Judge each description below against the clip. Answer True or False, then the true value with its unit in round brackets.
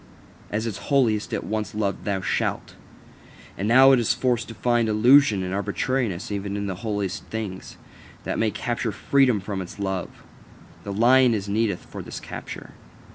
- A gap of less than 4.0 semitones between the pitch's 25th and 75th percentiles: True (3.0 semitones)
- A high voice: False (110 Hz)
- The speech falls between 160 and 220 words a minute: True (170 wpm)